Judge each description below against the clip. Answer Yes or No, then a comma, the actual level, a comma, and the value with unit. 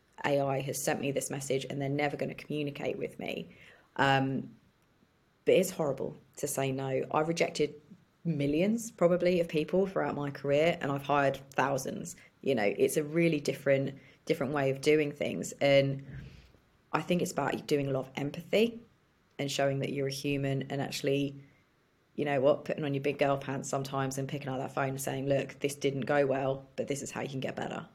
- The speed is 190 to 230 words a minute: Yes, average, 200 wpm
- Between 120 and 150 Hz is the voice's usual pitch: Yes, medium, 140 Hz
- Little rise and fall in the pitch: Yes, narrow, 1.6 semitones